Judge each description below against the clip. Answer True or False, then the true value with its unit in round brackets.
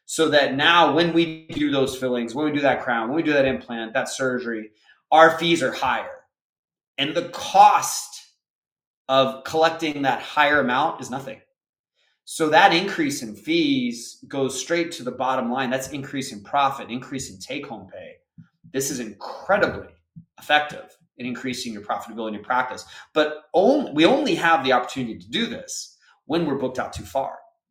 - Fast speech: False (175 wpm)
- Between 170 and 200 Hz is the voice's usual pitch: False (140 Hz)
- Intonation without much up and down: False (4.3 semitones)